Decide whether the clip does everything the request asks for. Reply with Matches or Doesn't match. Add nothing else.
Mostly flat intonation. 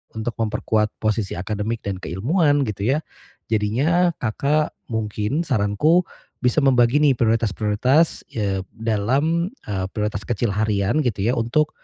Doesn't match